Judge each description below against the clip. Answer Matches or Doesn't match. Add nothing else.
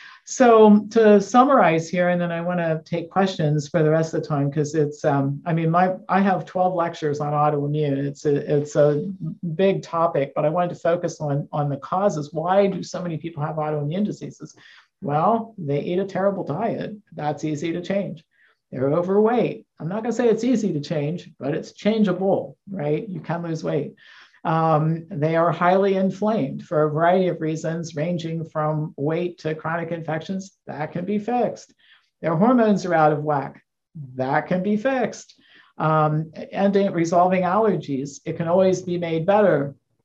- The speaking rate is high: Doesn't match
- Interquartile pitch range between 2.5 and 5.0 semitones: Matches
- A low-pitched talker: Doesn't match